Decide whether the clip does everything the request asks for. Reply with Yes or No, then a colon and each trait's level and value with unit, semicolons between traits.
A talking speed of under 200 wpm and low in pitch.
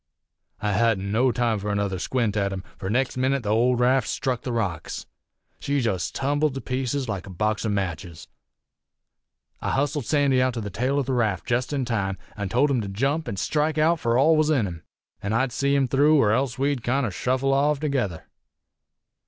No: fast, 205 wpm; low, 125 Hz